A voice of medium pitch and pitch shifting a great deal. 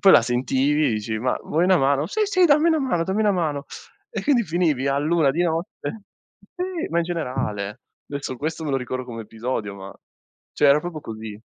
Yes: medium, 150 Hz; wide, 6.0 semitones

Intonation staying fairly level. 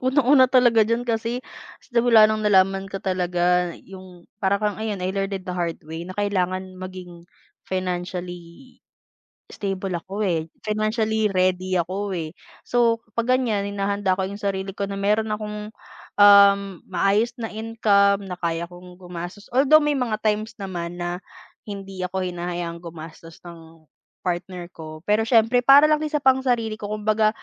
No: average, 3.5 semitones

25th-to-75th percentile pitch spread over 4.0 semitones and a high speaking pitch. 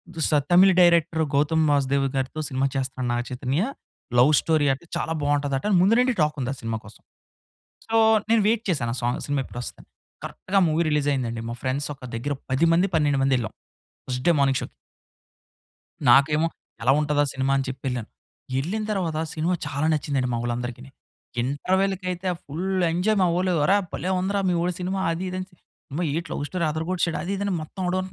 No: average, 5.1 semitones; medium, 150 Hz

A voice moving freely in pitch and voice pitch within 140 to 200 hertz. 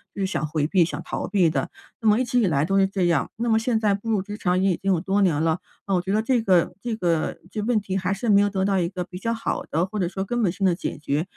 No: average, 3.2 semitones; high, 195 Hz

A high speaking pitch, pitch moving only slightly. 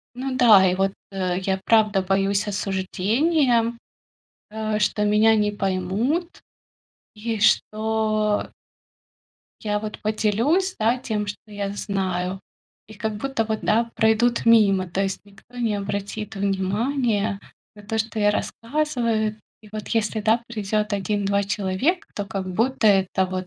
Yes: high, 210 Hz; narrow, 2.3 semitones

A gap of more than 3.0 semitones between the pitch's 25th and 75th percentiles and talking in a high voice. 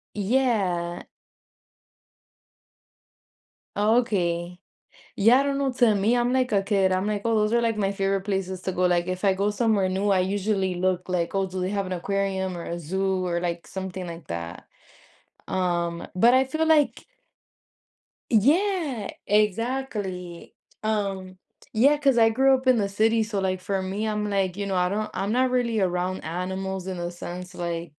Yes: average, 3.5 semitones; high, 195 Hz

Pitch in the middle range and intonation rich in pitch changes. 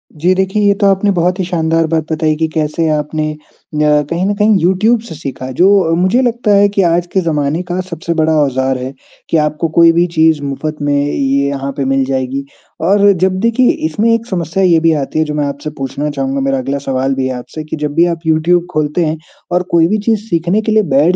No: medium, 160 Hz; average, 4.2 semitones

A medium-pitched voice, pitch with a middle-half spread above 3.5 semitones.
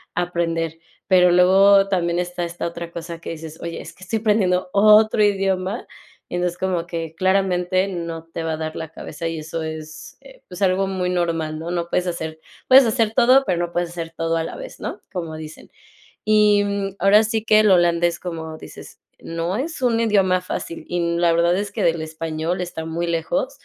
No: medium, 175 Hz; average, 2.9 semitones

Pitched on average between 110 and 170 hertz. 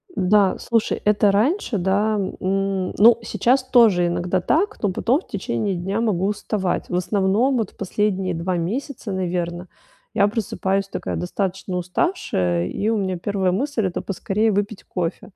No: high, 195 Hz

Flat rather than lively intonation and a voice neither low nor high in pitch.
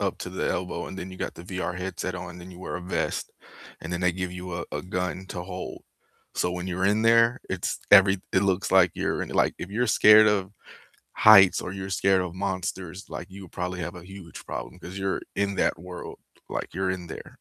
No: narrow, 1.4 semitones; very low, 95 Hz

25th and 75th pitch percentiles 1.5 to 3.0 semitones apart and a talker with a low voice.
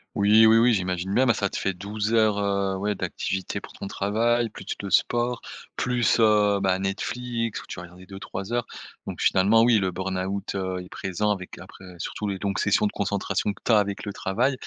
Yes: average, 2.7 semitones; low, 100 Hz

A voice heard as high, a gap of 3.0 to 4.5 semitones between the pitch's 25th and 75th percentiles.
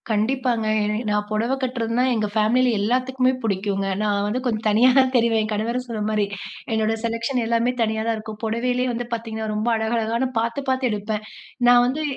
No: high, 230 Hz; narrow, 2.4 semitones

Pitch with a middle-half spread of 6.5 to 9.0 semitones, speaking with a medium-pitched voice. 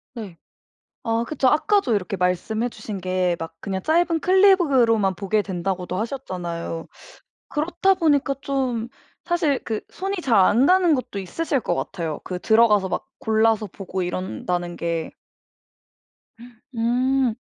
No: wide, 7.0 semitones; high, 225 Hz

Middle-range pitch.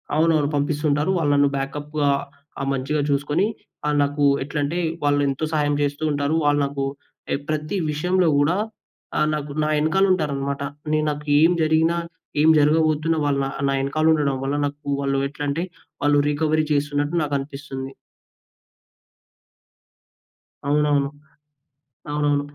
Yes: medium, 145 Hz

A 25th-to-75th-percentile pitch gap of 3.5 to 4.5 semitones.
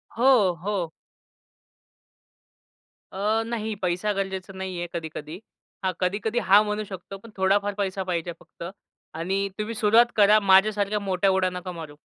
No: narrow, 2.4 semitones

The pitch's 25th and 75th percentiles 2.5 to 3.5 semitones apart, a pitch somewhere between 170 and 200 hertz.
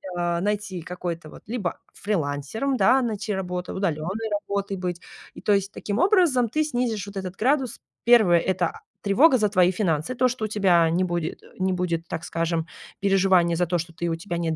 No: average, 4.0 semitones; high, 190 Hz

